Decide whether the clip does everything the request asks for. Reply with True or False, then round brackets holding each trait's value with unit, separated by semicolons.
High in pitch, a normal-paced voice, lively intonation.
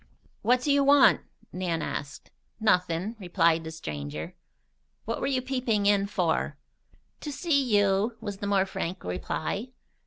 True (200 Hz; 145 wpm; 6.5 semitones)